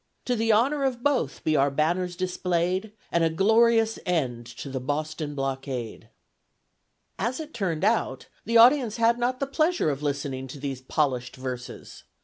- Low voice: No, medium, 170 Hz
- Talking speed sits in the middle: Yes, average, 160 wpm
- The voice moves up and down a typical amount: No, wide, 9.0 semitones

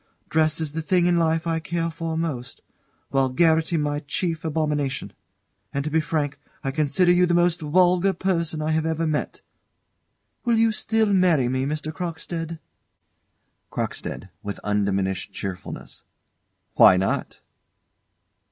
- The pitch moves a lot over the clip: No, average, 3.0 semitones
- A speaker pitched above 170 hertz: No, medium, 160 Hz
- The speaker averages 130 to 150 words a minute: Yes, slow, 135 wpm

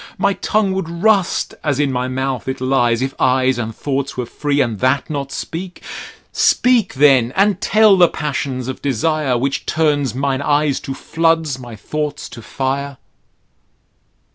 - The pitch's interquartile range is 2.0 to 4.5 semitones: Yes, average, 3.8 semitones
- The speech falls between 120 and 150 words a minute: No, average, 160 wpm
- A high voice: No, medium, 140 Hz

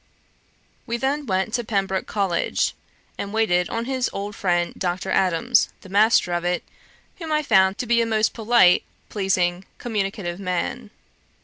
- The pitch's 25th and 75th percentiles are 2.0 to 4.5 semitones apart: Yes, average, 4.2 semitones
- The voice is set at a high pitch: Yes, high, 200 Hz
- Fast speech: No, average, 150 wpm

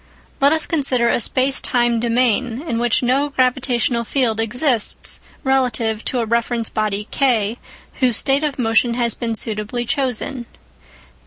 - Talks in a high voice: Yes, high, 240 Hz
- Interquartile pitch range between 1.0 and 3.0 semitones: Yes, narrow, 2.5 semitones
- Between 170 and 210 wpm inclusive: No, average, 145 wpm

